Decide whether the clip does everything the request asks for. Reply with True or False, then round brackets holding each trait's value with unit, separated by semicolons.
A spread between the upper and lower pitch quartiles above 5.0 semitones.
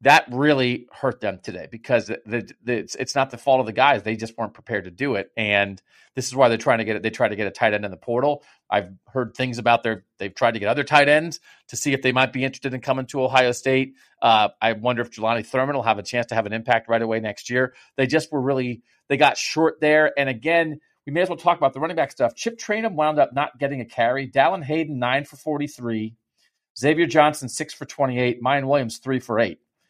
False (4.0 semitones)